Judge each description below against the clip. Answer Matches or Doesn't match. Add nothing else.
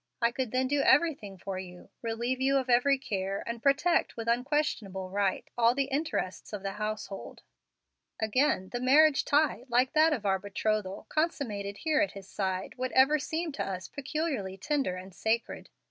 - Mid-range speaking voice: Doesn't match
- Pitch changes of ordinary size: Doesn't match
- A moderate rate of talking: Matches